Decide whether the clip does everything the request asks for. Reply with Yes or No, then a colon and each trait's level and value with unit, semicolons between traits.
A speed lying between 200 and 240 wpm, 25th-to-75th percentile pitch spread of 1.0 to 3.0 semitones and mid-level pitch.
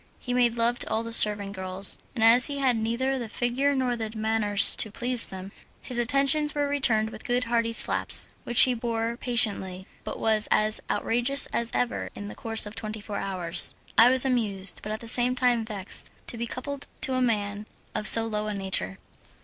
No: fast, 205 wpm; average, 2.7 semitones; high, 230 Hz